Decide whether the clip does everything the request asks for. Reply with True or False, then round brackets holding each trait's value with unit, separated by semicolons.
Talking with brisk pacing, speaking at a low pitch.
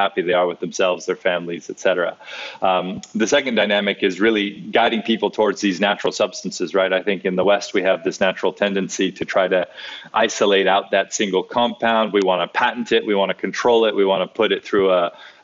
True (220 wpm; 100 Hz)